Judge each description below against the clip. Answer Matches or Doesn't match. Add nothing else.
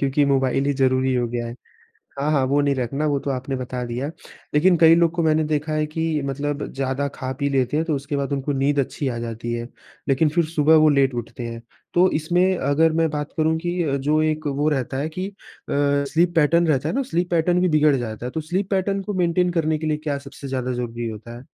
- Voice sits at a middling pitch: Matches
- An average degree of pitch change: Matches